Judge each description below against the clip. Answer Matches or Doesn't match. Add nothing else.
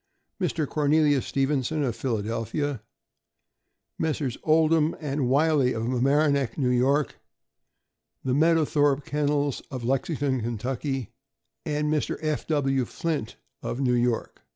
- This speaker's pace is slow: Matches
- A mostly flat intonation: Doesn't match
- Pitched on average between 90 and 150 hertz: Matches